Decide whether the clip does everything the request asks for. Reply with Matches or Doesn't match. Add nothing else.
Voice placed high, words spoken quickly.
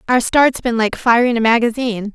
Doesn't match